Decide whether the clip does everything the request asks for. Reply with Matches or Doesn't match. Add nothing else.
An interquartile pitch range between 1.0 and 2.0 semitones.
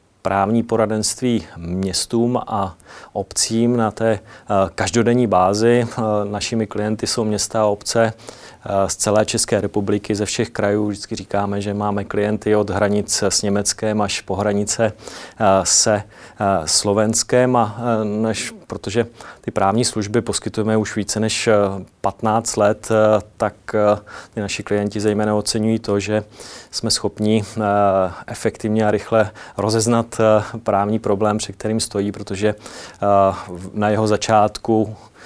Matches